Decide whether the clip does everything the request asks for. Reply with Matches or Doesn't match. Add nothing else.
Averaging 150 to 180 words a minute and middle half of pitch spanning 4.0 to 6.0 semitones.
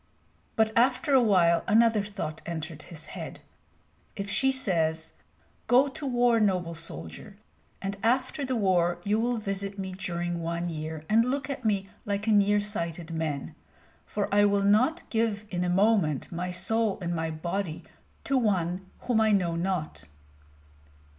Matches